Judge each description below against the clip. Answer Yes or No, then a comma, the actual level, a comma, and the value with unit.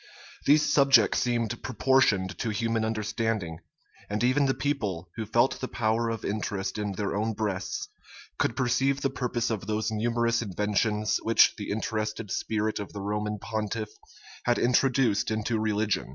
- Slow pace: No, average, 150 wpm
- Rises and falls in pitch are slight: Yes, narrow, 2.3 semitones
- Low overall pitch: Yes, low, 110 Hz